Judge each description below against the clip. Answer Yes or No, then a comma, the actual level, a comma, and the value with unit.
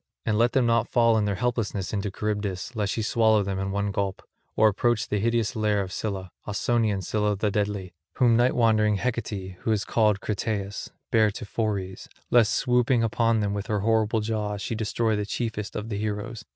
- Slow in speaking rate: No, average, 195 wpm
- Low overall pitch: Yes, low, 105 Hz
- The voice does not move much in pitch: Yes, narrow, 2.1 semitones